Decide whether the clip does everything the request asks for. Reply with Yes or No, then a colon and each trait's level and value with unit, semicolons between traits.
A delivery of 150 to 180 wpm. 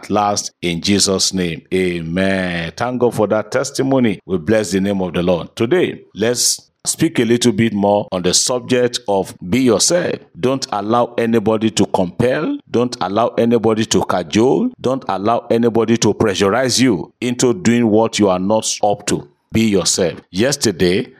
Yes: average, 160 wpm